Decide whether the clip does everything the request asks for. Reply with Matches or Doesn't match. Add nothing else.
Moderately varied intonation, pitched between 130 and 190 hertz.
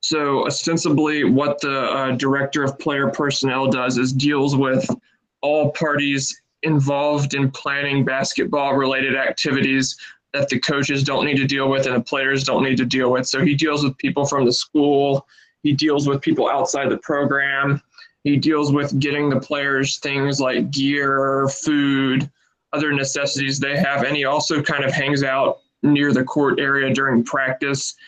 Doesn't match